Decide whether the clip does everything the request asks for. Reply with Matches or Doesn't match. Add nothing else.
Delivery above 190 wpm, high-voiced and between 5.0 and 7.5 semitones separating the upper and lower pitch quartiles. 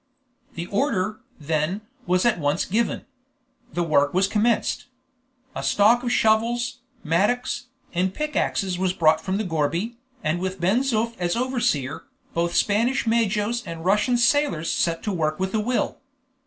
Doesn't match